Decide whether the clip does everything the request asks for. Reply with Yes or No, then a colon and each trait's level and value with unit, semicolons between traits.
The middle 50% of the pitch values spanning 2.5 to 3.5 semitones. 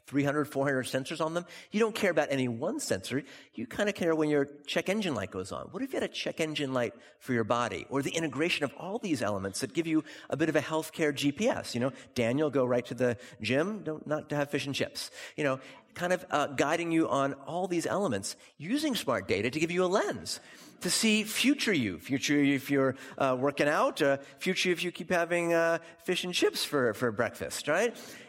No: average, 4.3 semitones